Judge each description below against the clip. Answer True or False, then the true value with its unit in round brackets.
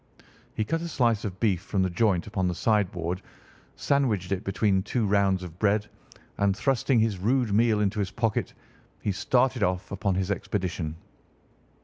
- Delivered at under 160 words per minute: False (165 wpm)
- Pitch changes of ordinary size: True (3.3 semitones)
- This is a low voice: True (100 Hz)